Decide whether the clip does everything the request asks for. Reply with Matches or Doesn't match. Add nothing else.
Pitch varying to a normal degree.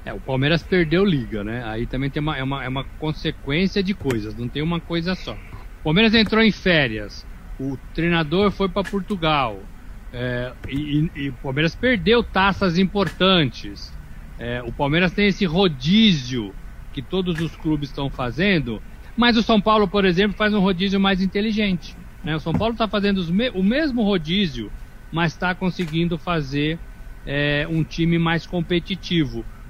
Doesn't match